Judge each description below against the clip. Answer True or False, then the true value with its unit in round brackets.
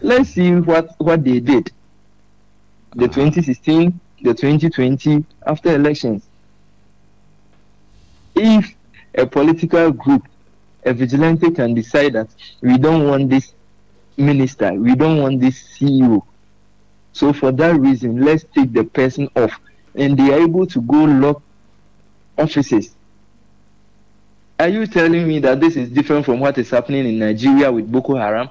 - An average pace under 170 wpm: True (135 wpm)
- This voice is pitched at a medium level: False (130 Hz)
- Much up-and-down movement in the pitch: True (6.5 semitones)